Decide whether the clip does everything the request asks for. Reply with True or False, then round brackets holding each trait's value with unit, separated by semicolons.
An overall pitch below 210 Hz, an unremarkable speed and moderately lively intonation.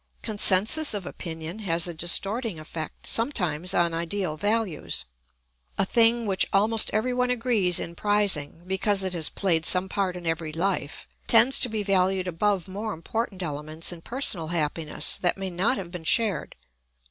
True (190 Hz; 160 wpm; 4.1 semitones)